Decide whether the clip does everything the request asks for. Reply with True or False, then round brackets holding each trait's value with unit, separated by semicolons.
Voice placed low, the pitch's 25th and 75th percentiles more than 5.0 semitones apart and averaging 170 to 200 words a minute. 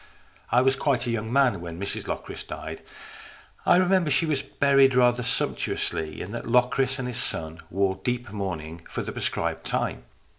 True (125 Hz; 5.5 semitones; 175 wpm)